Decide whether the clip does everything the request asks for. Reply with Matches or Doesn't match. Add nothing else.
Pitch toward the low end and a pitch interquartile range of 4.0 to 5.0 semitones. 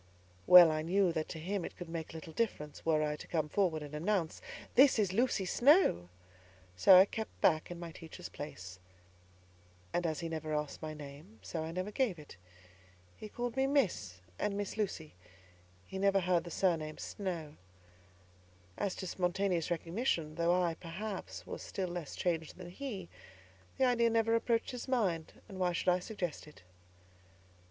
Doesn't match